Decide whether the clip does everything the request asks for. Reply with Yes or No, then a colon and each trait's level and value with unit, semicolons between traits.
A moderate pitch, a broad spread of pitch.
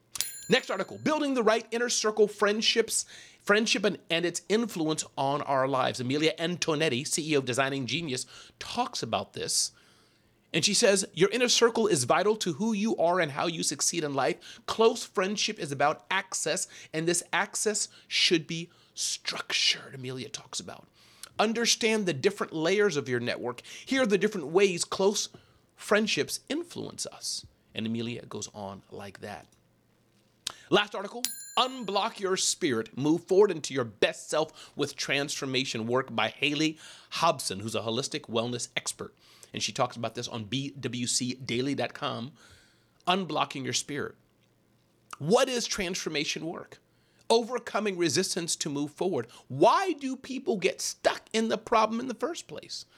Yes: medium, 175 Hz; wide, 8.4 semitones